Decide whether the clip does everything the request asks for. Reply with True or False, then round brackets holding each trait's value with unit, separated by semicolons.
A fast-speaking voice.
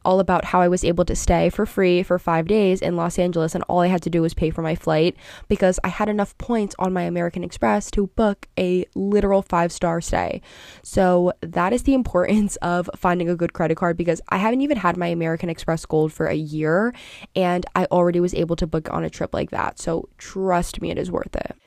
True (235 wpm)